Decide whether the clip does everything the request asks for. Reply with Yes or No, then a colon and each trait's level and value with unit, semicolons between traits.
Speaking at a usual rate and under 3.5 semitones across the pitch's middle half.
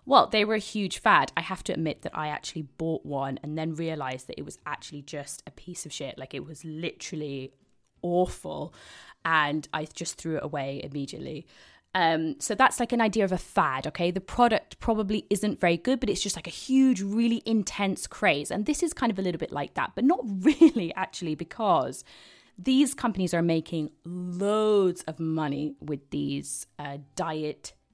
No: average, 195 wpm; wide, 5.6 semitones